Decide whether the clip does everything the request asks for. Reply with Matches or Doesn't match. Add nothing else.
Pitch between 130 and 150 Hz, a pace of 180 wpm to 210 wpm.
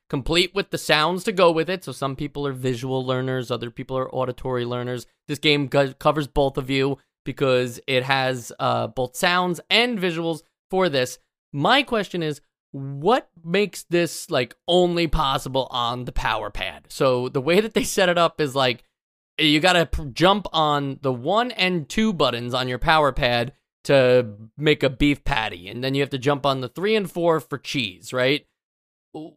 Matches